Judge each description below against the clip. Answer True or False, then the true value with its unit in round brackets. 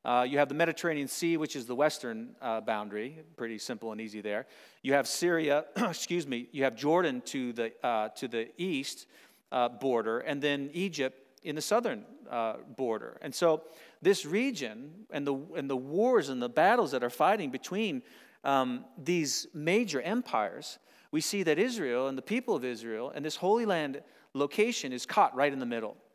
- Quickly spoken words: False (185 wpm)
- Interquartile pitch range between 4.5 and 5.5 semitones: True (5.2 semitones)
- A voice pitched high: False (150 Hz)